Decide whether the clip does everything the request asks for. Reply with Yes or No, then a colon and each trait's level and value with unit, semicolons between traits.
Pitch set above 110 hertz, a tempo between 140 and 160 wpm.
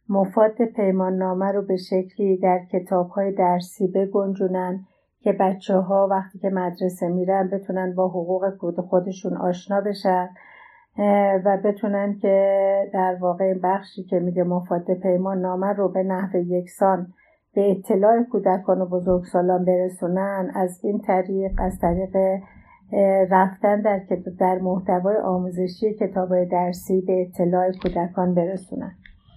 No: high, 190 Hz; average, 125 wpm